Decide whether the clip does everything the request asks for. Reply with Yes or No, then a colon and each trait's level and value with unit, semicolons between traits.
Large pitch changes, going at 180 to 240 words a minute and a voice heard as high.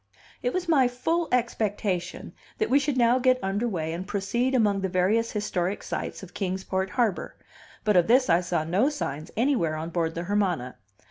Yes: wide, 5.7 semitones; average, 190 wpm; high, 200 Hz